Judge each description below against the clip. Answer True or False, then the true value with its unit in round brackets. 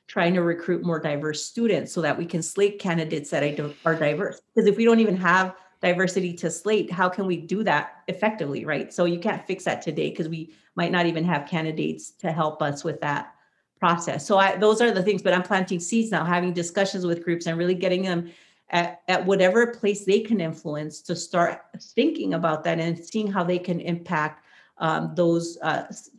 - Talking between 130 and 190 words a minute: False (205 wpm)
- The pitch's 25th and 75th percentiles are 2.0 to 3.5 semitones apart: True (2.8 semitones)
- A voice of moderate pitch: True (175 Hz)